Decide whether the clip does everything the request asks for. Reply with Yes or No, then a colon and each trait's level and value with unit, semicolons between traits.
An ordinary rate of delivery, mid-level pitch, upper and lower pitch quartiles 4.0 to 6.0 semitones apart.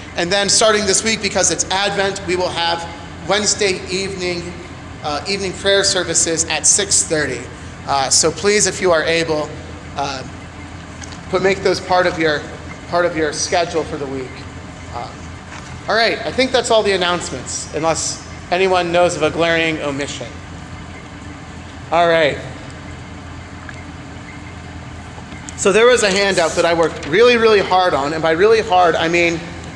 Yes: average, 155 wpm; medium, 170 Hz; average, 5.0 semitones